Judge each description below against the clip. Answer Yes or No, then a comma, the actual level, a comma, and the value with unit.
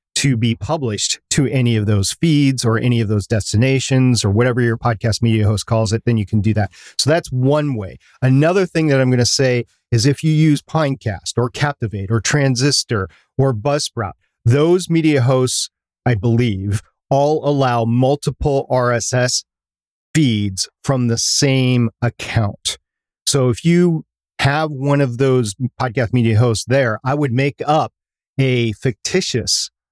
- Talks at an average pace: Yes, average, 160 wpm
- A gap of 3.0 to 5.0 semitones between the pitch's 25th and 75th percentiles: Yes, average, 3.6 semitones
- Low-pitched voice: Yes, low, 125 Hz